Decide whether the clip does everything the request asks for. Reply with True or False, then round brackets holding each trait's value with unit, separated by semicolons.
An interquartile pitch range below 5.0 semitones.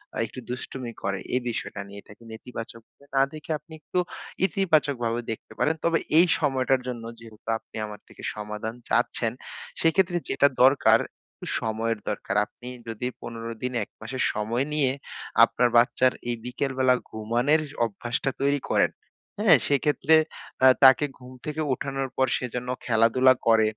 True (3.8 semitones)